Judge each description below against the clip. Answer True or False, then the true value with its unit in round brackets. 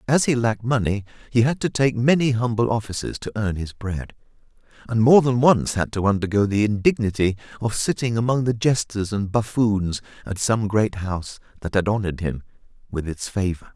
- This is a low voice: True (110 Hz)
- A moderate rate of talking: True (185 wpm)